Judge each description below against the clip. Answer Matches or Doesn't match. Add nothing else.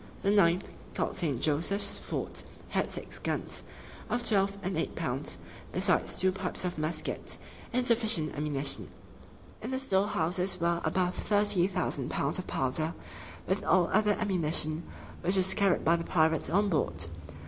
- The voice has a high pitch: Doesn't match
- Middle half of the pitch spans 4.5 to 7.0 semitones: Doesn't match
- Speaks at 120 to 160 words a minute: Matches